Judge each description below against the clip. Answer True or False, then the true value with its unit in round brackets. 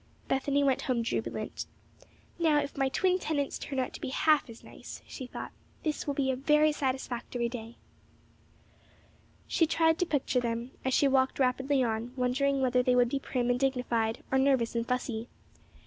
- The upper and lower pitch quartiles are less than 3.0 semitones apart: True (2.4 semitones)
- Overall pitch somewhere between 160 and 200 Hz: False (260 Hz)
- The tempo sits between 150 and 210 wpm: True (180 wpm)